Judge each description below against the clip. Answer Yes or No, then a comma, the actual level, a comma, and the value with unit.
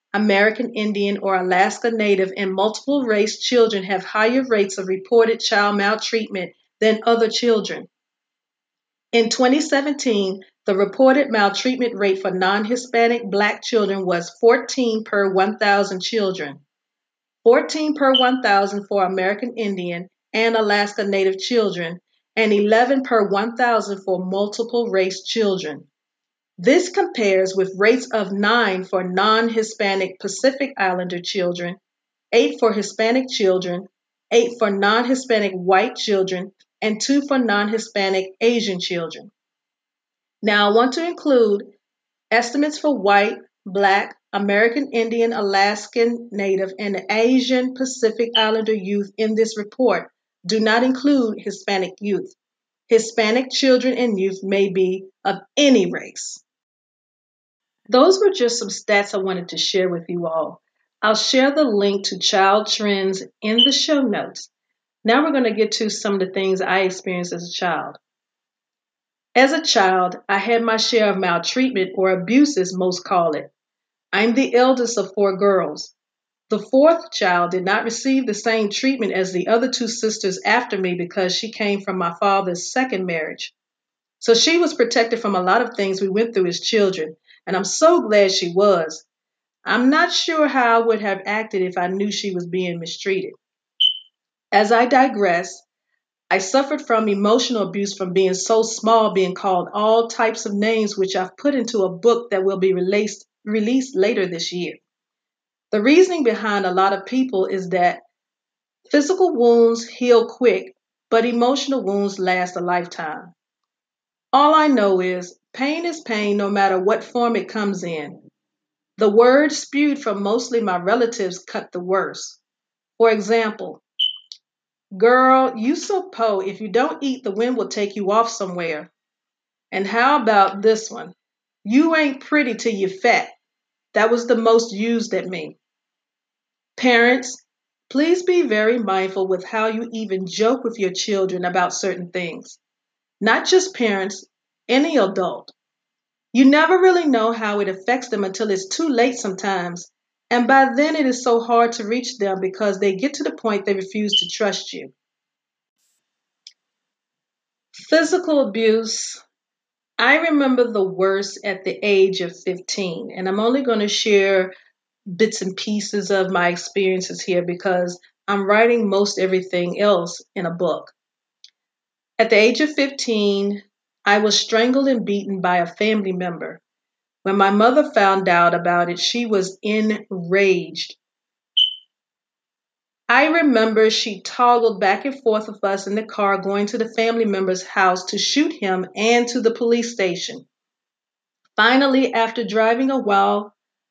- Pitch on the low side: No, high, 215 Hz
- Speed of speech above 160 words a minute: No, average, 150 wpm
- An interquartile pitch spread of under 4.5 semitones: Yes, average, 3.7 semitones